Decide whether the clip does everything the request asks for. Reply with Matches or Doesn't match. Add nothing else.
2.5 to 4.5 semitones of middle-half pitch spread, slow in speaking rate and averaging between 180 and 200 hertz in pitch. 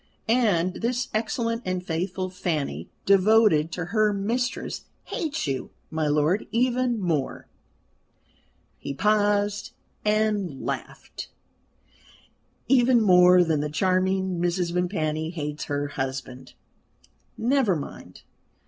Doesn't match